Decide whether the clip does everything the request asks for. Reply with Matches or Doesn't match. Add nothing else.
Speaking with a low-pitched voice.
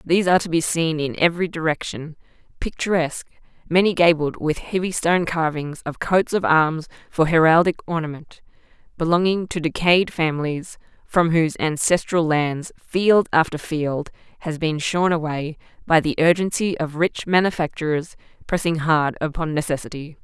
Doesn't match